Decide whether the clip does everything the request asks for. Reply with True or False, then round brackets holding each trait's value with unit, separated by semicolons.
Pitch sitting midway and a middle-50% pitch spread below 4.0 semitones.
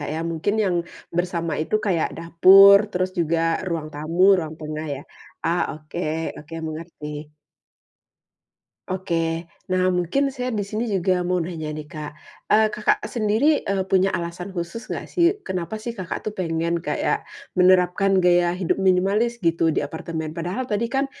True (180 Hz; 3.3 semitones)